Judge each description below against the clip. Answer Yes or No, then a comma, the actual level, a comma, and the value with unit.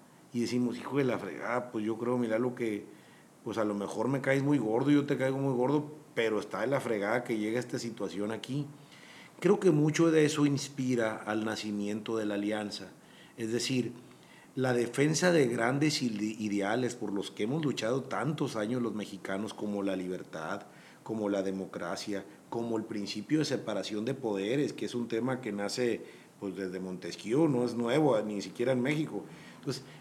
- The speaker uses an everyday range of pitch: Yes, average, 4.1 semitones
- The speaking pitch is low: Yes, low, 115 Hz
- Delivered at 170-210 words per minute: Yes, average, 185 wpm